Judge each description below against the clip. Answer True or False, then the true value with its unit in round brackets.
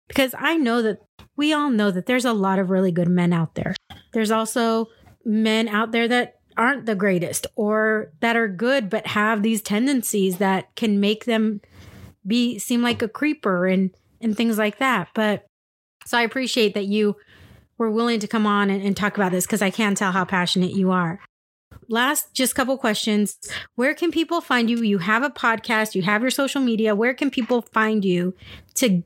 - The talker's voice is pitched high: True (220 Hz)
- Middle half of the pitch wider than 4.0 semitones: False (3.3 semitones)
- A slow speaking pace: False (200 wpm)